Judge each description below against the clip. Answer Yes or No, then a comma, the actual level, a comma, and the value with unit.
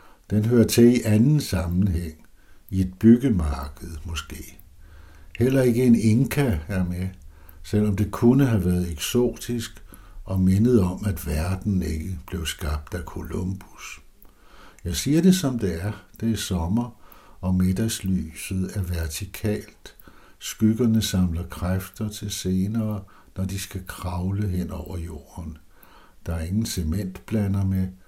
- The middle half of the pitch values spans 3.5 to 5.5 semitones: Yes, average, 3.8 semitones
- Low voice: Yes, very low, 95 Hz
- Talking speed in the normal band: No, slow, 130 wpm